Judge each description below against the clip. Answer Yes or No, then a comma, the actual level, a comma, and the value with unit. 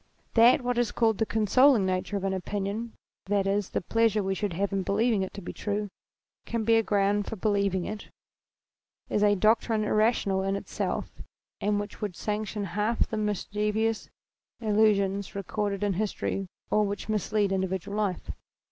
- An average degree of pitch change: No, narrow, 1.7 semitones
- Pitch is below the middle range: No, high, 205 Hz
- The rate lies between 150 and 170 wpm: Yes, average, 165 wpm